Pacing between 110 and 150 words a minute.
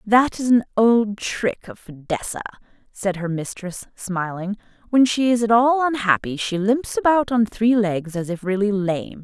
No: average, 175 wpm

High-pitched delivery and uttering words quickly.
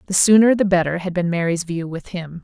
No: medium, 180 Hz; fast, 245 wpm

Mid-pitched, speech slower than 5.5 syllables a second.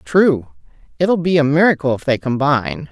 Yes: medium, 155 Hz; 5.1 syllables/s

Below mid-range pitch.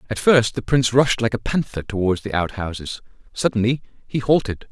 Yes: low, 115 Hz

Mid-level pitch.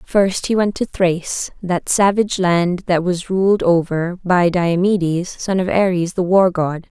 Yes: medium, 180 Hz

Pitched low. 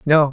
No: medium, 150 Hz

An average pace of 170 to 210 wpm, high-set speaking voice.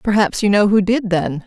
No: fast, 245 wpm; high, 200 Hz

